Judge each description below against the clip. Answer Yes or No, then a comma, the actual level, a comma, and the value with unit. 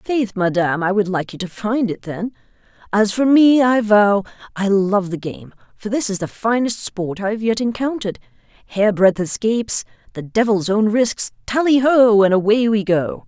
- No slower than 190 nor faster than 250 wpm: No, average, 175 wpm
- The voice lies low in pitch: No, high, 210 Hz